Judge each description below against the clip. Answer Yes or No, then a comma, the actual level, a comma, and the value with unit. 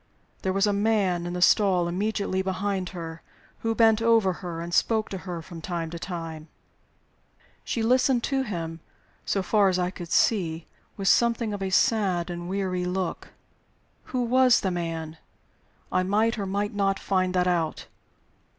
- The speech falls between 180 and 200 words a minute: No, average, 170 wpm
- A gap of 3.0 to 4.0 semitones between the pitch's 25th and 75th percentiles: Yes, average, 3.4 semitones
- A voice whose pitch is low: No, high, 190 Hz